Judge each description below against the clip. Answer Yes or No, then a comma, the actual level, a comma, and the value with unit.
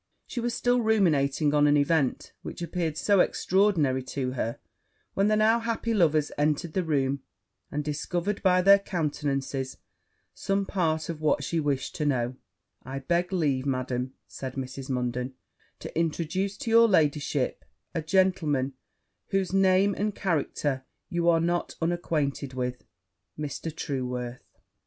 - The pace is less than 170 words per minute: Yes, average, 140 wpm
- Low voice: No, medium, 155 Hz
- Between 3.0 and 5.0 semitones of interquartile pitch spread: No, wide, 5.5 semitones